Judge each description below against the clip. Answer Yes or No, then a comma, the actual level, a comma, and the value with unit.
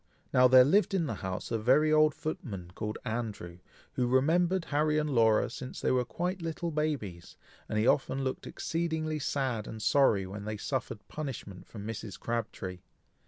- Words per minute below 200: Yes, average, 170 wpm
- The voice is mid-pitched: No, low, 130 Hz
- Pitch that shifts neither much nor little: No, wide, 6.1 semitones